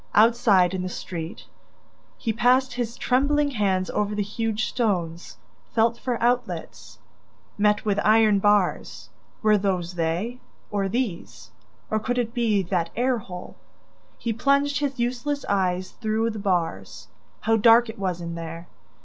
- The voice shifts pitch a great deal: No, average, 4.5 semitones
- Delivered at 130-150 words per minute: Yes, average, 145 wpm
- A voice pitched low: No, high, 210 Hz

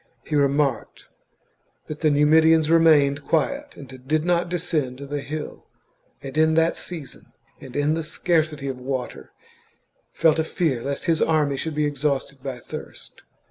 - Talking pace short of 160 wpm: Yes, average, 150 wpm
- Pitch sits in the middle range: Yes, medium, 150 Hz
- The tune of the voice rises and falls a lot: No, average, 2.7 semitones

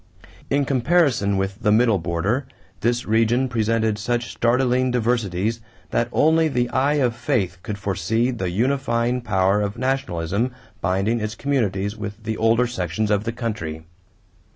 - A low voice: Yes, low, 115 Hz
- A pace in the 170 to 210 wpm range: No, average, 145 wpm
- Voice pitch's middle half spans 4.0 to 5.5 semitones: No, average, 3.6 semitones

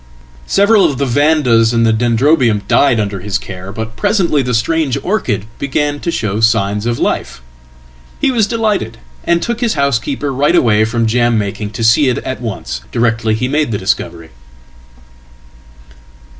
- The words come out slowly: No, average, 150 wpm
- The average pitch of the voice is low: Yes, low, 120 Hz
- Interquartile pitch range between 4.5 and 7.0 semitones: Yes, average, 5.2 semitones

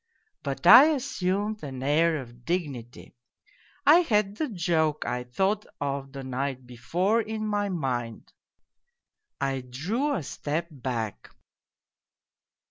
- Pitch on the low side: No, medium, 155 Hz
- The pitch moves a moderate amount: No, wide, 7.9 semitones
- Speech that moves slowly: Yes, slow, 120 wpm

